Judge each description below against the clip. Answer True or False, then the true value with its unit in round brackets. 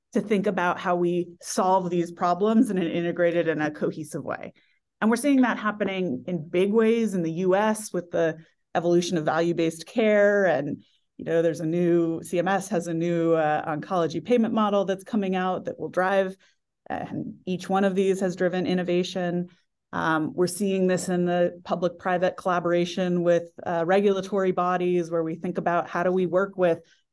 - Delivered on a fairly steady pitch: True (2.0 semitones)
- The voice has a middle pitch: True (180 Hz)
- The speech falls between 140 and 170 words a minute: False (180 wpm)